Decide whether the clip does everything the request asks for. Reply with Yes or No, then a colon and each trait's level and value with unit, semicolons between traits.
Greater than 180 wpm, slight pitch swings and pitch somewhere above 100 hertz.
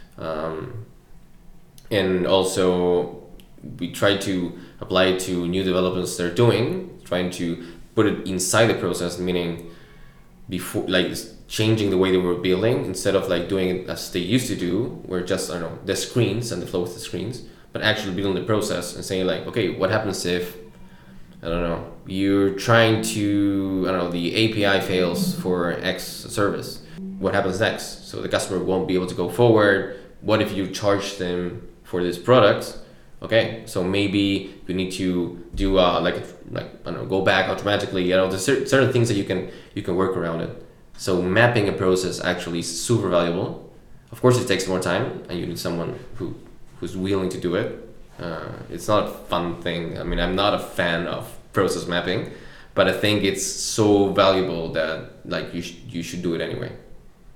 No: average, 190 wpm; narrow, 2.2 semitones; very low, 95 Hz